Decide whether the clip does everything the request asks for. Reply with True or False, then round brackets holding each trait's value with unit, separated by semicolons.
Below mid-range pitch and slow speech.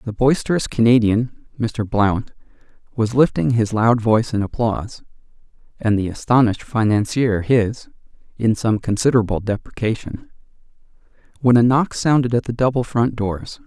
True (115 Hz; 130 wpm)